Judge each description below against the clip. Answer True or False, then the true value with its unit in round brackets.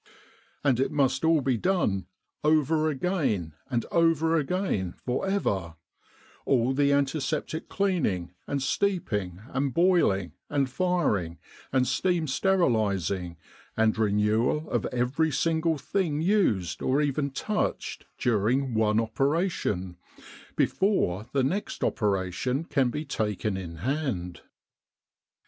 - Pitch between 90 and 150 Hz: True (135 Hz)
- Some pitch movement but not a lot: False (7.3 semitones)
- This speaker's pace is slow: True (120 wpm)